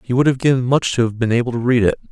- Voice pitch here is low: Yes, low, 125 Hz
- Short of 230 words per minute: No, fast, 340 wpm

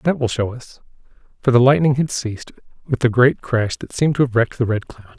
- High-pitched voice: No, low, 120 Hz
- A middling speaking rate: No, fast, 245 wpm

